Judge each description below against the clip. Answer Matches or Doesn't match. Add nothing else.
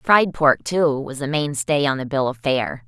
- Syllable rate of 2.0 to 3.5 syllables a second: Doesn't match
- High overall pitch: Doesn't match